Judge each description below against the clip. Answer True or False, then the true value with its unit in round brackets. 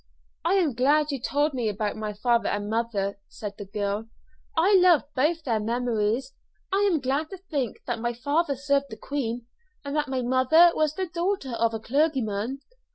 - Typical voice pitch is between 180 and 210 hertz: False (260 Hz)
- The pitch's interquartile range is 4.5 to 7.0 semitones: True (5.3 semitones)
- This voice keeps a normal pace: True (185 wpm)